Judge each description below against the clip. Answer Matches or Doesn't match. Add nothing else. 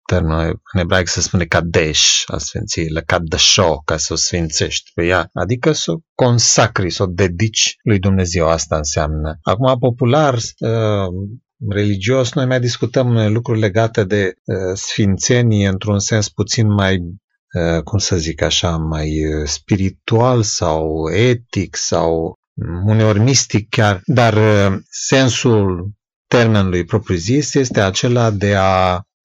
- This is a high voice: Doesn't match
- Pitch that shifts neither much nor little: Matches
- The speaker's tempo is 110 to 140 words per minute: Matches